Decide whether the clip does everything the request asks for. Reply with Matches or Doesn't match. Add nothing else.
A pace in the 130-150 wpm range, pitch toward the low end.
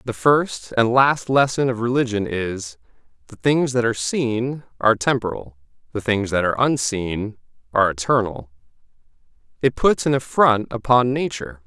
Matches